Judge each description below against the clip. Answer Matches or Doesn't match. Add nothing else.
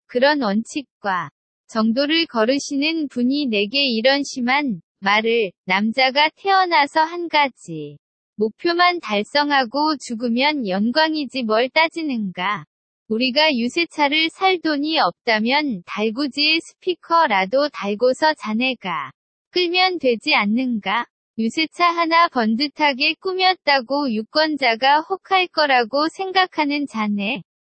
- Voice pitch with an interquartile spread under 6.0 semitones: Matches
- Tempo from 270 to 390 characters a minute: Doesn't match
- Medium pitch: Doesn't match